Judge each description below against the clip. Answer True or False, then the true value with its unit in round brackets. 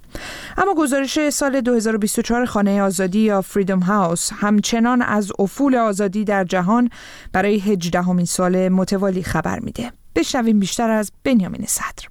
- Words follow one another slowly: False (130 wpm)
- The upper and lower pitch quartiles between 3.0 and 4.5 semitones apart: True (3.6 semitones)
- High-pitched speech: True (210 Hz)